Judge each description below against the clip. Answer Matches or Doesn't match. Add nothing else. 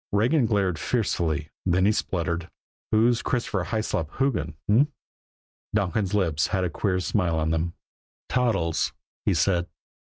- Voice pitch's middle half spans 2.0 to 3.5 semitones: Doesn't match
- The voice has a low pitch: Matches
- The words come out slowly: Matches